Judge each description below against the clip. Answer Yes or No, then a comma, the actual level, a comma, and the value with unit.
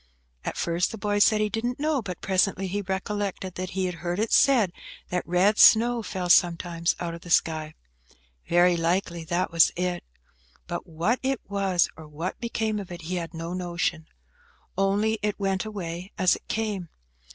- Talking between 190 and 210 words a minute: No, average, 180 wpm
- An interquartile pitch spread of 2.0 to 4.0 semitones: Yes, average, 3.2 semitones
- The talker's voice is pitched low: No, medium, 185 Hz